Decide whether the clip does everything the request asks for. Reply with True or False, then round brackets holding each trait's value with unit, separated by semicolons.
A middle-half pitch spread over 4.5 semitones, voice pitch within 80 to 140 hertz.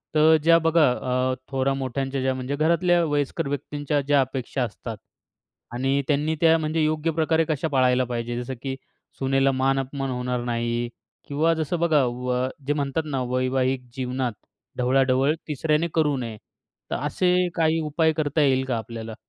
False (3.3 semitones; 135 Hz)